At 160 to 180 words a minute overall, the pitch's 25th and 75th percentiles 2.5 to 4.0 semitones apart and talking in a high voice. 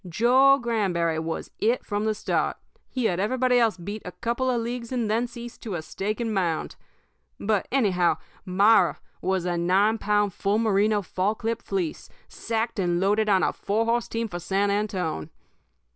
Yes: average, 175 wpm; average, 3.6 semitones; high, 210 Hz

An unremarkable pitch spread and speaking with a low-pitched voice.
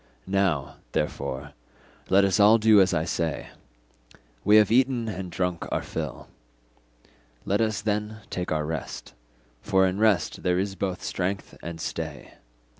Yes: average, 3.9 semitones; very low, 95 Hz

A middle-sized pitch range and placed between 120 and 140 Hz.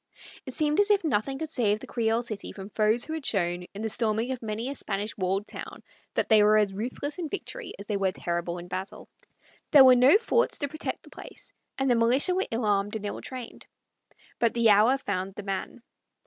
No: average, 4.8 semitones; high, 225 Hz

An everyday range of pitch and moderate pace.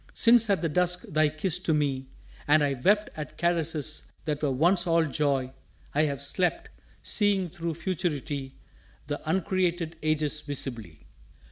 Yes: average, 3.7 semitones; average, 145 wpm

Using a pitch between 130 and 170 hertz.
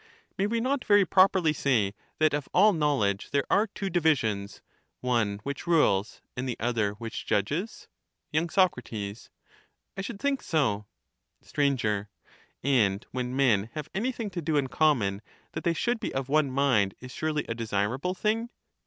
Yes: medium, 140 Hz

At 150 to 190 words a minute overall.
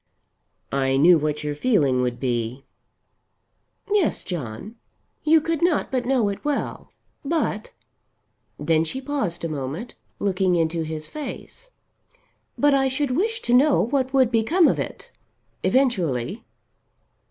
No: slow, 135 wpm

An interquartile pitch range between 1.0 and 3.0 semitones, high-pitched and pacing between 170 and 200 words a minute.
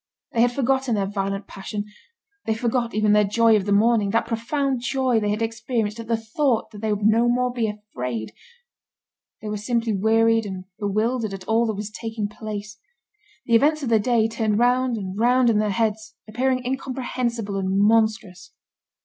Yes: narrow, 2.4 semitones; high, 220 Hz; average, 185 wpm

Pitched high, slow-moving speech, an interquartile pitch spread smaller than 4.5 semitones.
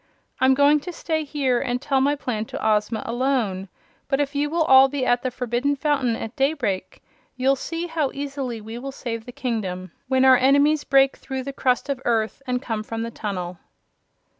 No: very high, 260 Hz; average, 195 wpm; average, 3.6 semitones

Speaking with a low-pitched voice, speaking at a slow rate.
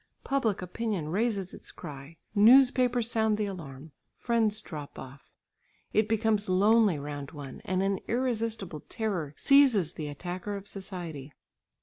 No: high, 200 Hz; slow, 130 wpm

